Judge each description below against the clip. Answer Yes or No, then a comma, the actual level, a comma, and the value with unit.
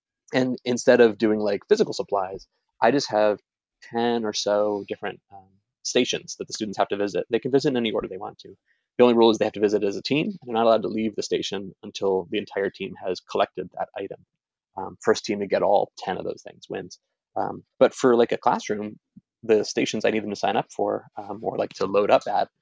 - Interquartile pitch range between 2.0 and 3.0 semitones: Yes, narrow, 2.4 semitones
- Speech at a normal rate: No, fast, 240 wpm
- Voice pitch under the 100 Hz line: No, low, 110 Hz